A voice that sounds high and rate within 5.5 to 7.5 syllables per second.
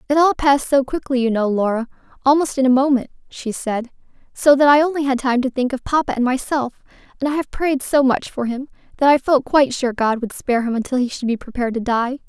Yes: very high, 260 Hz; 6.1 syllables/s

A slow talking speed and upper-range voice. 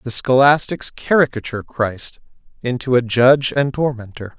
No: slow, 125 wpm; low, 125 Hz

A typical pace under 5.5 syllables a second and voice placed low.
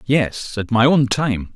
Yes: 3.5 syllables/s; low, 120 Hz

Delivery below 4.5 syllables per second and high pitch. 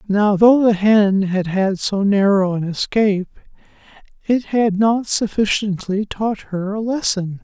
Yes: 4.0 syllables/s; high, 205 Hz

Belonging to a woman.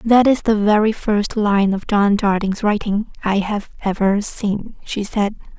Yes: female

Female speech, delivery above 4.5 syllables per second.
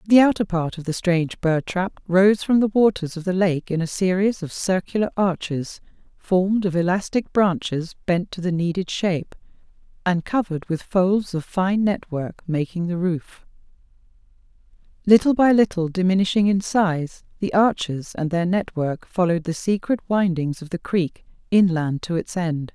Yes: female; 4.8 syllables/s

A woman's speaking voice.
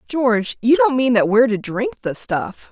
Yes: female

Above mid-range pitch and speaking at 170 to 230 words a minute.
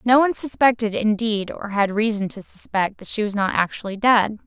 Yes: high, 215 Hz; average, 200 wpm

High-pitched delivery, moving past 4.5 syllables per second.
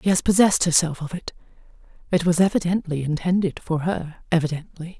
No: medium, 170 Hz; 5.9 syllables/s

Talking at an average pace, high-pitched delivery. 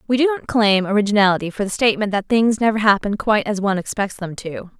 No: fast, 225 wpm; high, 210 Hz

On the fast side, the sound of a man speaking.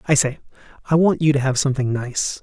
Yes: fast, 225 wpm; male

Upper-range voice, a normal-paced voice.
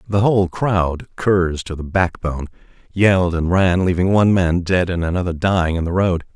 No: very low, 90 Hz; average, 170 wpm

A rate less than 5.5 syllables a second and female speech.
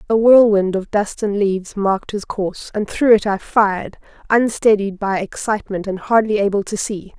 Yes: 5.1 syllables/s; female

